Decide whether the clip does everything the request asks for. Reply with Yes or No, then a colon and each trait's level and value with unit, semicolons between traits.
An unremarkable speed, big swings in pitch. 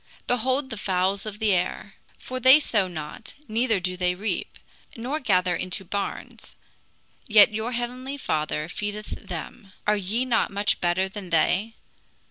No: average, 150 wpm; average, 4.5 semitones